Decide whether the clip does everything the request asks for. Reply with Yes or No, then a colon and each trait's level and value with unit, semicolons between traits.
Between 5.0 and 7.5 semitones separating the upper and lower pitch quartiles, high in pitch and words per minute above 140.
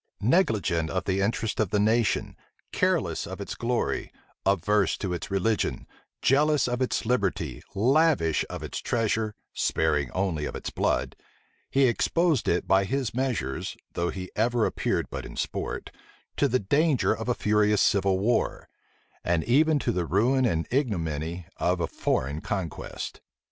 No: average, 5.3 semitones; low, 105 Hz; average, 155 wpm